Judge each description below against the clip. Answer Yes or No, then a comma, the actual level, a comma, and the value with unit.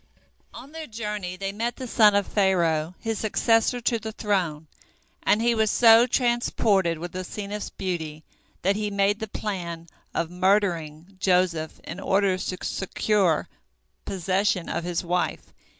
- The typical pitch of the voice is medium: No, high, 195 Hz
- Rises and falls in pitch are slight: No, average, 3.5 semitones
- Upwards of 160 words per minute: No, average, 145 wpm